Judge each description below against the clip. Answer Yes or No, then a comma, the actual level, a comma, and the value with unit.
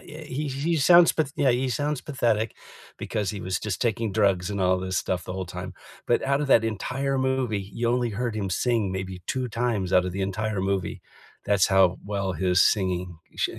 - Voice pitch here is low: Yes, low, 105 Hz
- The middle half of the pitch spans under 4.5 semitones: No, average, 5.0 semitones